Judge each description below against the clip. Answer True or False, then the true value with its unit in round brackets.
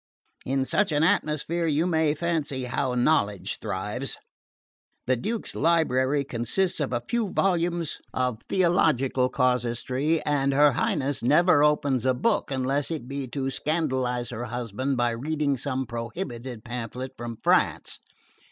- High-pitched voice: False (135 Hz)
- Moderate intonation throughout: True (4.0 semitones)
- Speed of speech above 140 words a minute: False (135 wpm)